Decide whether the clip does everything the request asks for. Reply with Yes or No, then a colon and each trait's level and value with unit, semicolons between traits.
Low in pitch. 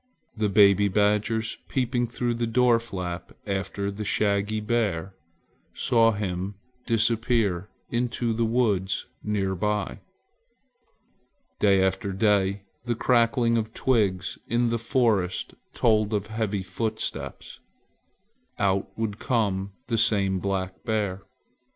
Yes: low, 105 Hz